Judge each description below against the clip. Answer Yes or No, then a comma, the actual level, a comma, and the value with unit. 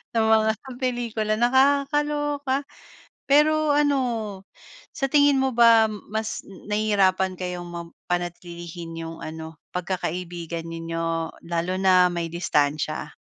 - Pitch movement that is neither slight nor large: No, wide, 7.0 semitones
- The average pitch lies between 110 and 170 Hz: No, high, 190 Hz